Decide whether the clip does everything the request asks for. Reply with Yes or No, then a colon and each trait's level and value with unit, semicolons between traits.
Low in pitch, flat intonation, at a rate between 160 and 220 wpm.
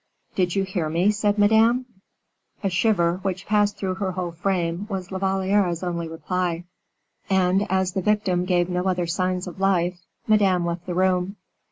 No: medium, 185 Hz; narrow, 1.8 semitones; average, 170 wpm